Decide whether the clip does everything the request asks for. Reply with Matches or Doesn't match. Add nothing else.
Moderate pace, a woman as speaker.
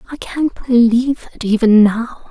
Matches